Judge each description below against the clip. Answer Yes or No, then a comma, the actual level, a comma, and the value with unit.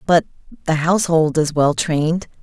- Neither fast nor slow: Yes, average, 150 wpm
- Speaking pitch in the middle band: Yes, medium, 160 Hz